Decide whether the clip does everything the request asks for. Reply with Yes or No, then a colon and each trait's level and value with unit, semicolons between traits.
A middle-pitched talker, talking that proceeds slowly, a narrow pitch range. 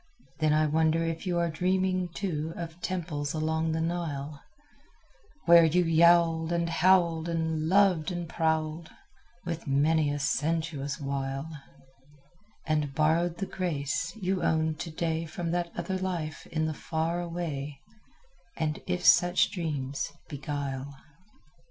Yes: medium, 160 Hz; slow, 130 wpm; narrow, 2.0 semitones